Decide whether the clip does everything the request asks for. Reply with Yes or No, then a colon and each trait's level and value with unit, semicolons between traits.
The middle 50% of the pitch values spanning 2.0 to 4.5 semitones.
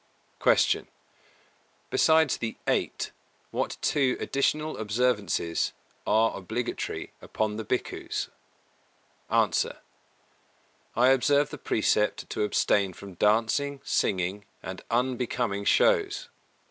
No: average, 4.9 semitones